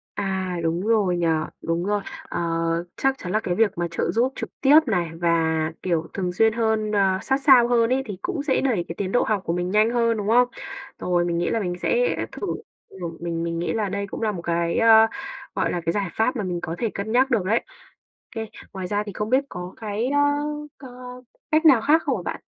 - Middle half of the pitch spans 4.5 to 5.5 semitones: Yes, average, 5.1 semitones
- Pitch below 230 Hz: Yes, high, 210 Hz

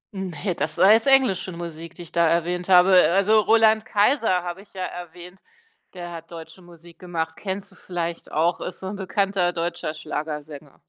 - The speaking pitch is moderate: Yes, medium, 175 Hz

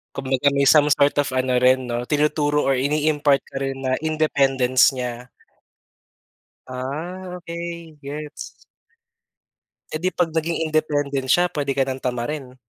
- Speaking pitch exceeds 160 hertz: No, medium, 145 Hz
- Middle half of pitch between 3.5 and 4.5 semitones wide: No, average, 3.0 semitones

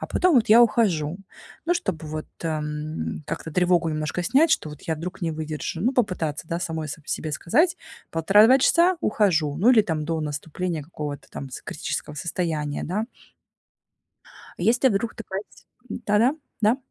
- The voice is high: No, medium, 170 Hz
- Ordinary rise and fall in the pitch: No, wide, 6.4 semitones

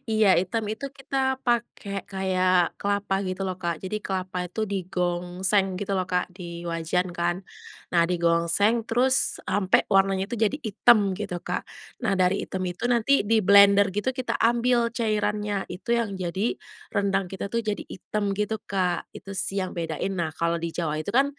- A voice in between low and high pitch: No, high, 195 Hz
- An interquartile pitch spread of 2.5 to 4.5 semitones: Yes, average, 2.8 semitones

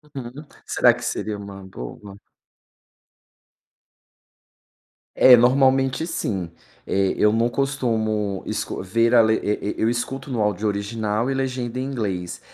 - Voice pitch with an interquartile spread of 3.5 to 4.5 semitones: Yes, average, 3.9 semitones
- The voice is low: Yes, low, 115 Hz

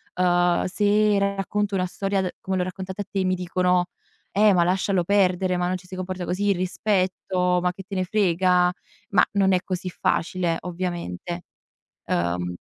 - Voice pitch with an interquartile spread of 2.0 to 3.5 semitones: No, narrow, 1.5 semitones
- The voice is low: No, medium, 185 Hz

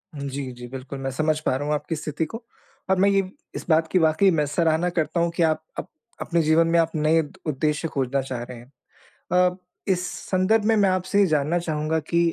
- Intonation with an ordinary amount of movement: Yes, average, 3.6 semitones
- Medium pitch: Yes, medium, 160 Hz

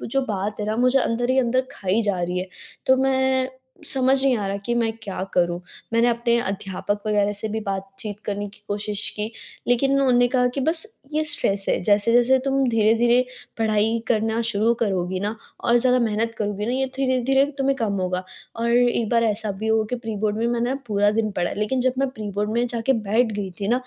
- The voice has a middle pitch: No, high, 225 Hz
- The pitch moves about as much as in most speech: Yes, average, 3.3 semitones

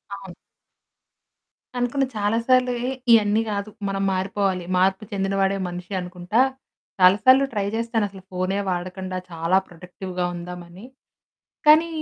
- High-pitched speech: Yes, high, 195 Hz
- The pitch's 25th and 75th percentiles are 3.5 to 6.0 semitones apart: No, average, 3.1 semitones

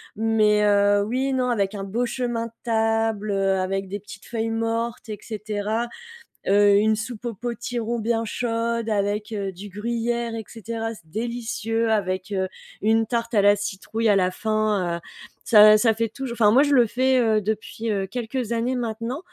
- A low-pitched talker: No, high, 225 Hz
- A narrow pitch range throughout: Yes, narrow, 2.2 semitones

